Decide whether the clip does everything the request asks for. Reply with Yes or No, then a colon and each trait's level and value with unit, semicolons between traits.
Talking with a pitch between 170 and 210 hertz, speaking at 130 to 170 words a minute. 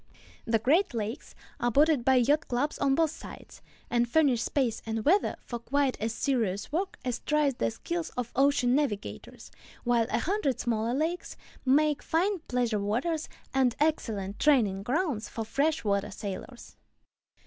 No: very high, 255 Hz; average, 155 wpm